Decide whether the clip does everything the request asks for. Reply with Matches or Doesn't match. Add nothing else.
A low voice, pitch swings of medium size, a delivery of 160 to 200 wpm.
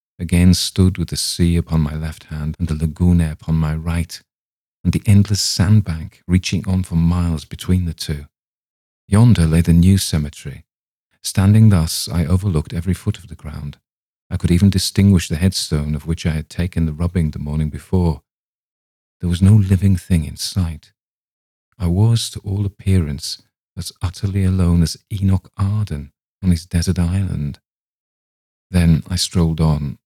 Matches